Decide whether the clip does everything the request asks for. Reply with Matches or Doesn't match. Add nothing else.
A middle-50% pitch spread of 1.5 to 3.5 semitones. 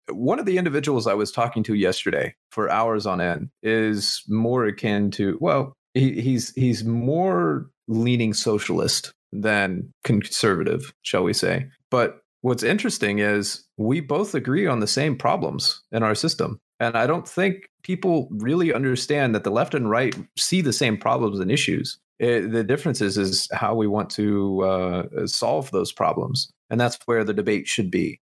Doesn't match